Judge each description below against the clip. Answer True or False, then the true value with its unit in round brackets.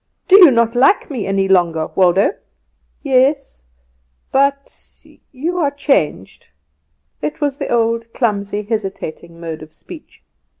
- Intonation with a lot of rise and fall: True (7.1 semitones)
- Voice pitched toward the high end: True (230 Hz)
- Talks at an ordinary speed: False (125 wpm)